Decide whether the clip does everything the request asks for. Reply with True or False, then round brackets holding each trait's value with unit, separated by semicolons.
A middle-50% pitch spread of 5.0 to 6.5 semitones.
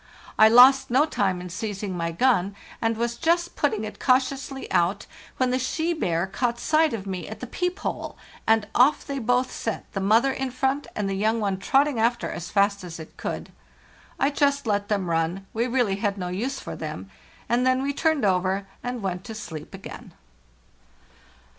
True (5.3 semitones)